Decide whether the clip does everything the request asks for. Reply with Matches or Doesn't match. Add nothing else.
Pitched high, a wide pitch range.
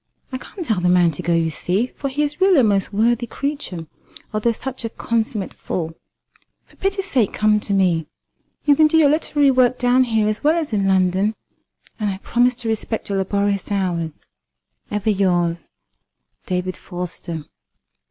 Matches